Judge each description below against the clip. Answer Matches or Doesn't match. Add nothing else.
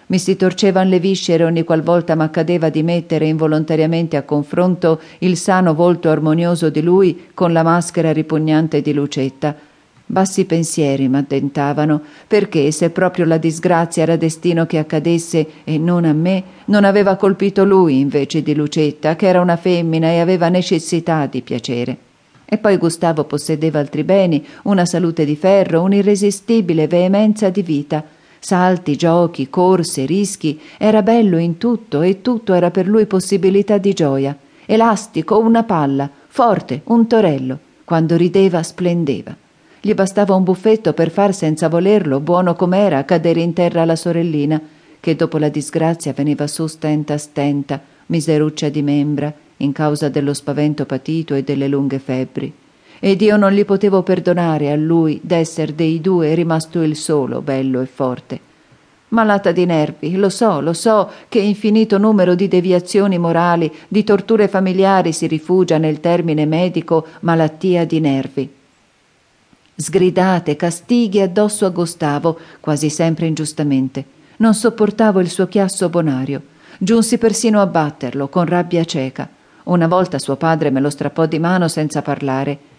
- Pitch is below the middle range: Doesn't match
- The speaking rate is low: Doesn't match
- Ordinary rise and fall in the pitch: Matches